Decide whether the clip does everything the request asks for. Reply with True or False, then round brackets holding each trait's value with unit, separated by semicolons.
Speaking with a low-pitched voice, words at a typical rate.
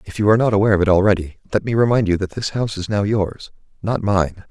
False (100 Hz; 265 wpm)